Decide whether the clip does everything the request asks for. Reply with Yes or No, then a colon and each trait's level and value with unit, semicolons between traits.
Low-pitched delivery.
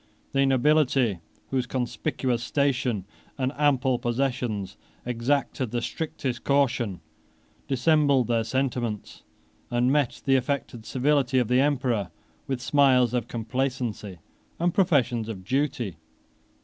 Yes: low, 125 Hz